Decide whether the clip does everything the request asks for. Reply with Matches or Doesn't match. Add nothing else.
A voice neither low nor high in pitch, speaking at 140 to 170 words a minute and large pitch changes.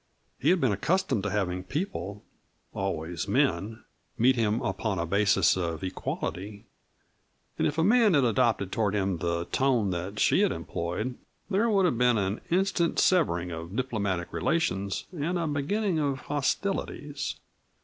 Doesn't match